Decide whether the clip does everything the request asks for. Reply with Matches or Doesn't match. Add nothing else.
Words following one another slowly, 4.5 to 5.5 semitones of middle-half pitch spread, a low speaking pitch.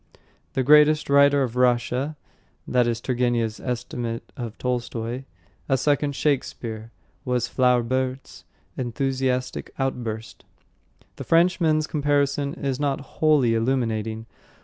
Doesn't match